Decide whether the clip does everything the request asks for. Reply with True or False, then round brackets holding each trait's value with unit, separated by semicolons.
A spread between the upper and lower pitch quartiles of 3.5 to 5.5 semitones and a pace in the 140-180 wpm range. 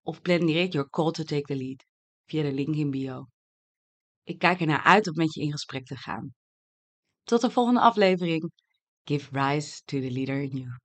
False (3.9 semitones; 200 wpm)